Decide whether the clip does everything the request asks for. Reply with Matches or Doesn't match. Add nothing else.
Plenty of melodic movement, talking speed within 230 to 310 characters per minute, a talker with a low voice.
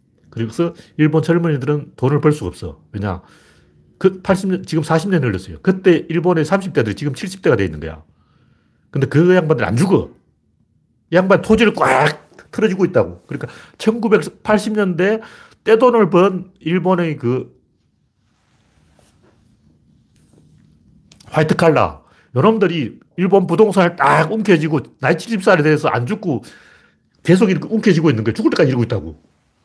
Doesn't match